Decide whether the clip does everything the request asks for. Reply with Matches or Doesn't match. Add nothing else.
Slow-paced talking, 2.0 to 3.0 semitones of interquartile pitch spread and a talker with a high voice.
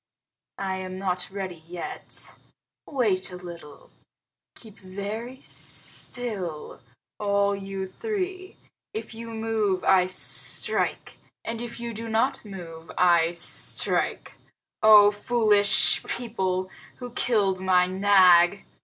Doesn't match